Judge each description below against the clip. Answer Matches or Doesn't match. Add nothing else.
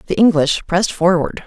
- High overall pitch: Doesn't match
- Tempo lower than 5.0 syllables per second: Doesn't match